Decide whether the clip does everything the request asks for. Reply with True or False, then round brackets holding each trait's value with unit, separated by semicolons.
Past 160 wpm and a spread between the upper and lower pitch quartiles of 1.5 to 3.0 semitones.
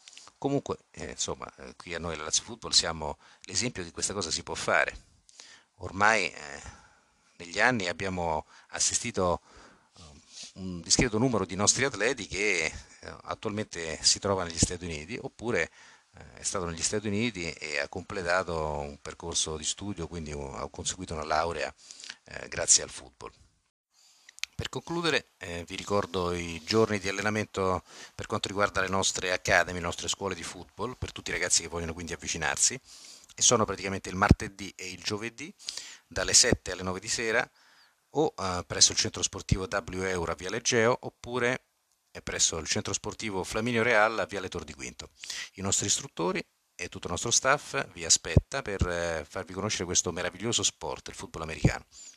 False (170 wpm; 3.7 semitones)